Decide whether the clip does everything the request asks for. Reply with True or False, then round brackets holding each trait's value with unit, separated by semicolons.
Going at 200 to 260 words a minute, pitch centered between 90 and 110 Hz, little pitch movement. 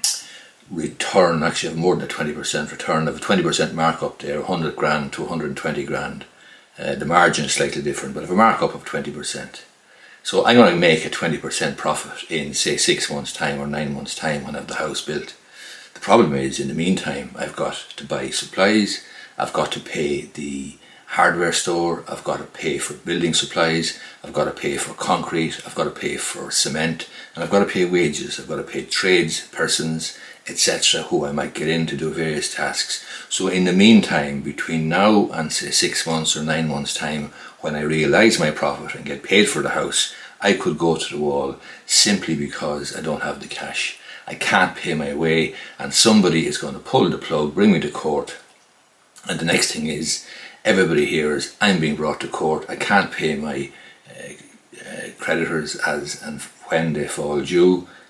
False (205 wpm; 80 Hz; 2.2 semitones)